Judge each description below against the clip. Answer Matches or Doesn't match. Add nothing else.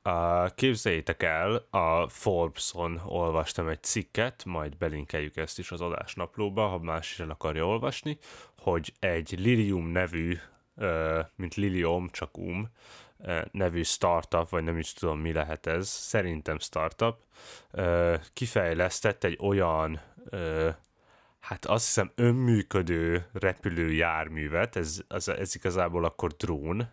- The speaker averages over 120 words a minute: Doesn't match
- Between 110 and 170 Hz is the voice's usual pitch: Doesn't match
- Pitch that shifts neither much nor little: Matches